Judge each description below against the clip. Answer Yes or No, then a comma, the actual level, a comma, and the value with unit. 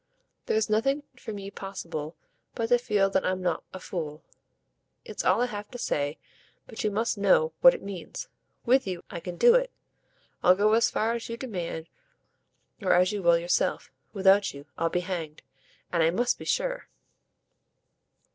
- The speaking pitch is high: Yes, high, 195 Hz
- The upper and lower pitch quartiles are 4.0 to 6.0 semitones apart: Yes, average, 4.6 semitones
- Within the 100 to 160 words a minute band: No, average, 175 wpm